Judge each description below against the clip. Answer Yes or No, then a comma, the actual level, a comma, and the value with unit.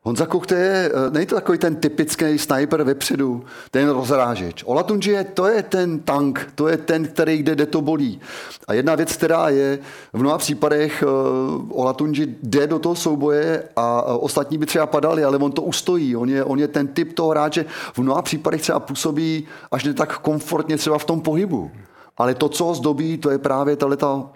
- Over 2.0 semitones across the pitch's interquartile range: Yes, narrow, 2.5 semitones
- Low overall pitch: No, medium, 150 Hz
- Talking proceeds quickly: Yes, fast, 190 wpm